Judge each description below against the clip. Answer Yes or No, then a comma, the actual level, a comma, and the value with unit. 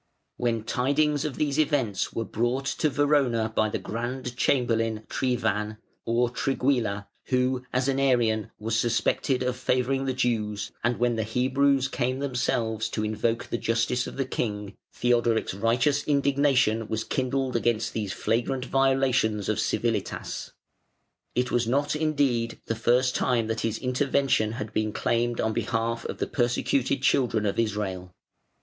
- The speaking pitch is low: Yes, low, 120 Hz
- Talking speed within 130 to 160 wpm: Yes, average, 150 wpm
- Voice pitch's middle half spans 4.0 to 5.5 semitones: No, average, 3.0 semitones